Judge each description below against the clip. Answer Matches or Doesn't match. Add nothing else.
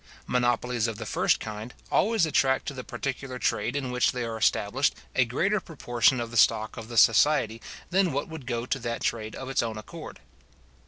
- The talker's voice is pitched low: Matches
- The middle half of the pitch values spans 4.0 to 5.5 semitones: Doesn't match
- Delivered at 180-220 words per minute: Matches